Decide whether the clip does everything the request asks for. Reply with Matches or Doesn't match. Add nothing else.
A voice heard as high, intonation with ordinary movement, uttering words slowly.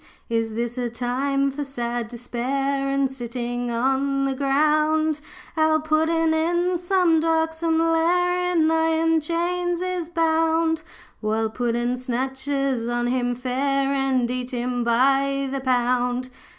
Matches